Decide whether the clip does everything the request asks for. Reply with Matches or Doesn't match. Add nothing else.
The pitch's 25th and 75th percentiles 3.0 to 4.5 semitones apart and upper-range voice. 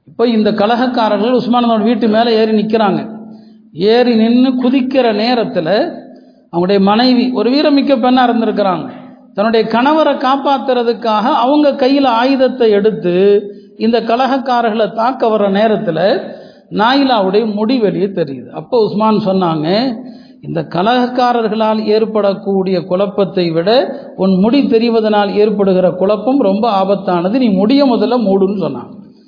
Matches